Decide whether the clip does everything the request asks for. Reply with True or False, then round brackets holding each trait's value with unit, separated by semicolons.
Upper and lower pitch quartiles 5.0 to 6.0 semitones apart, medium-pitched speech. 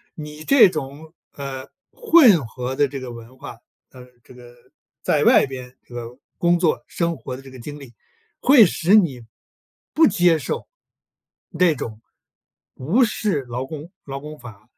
True (5.3 semitones; 145 Hz)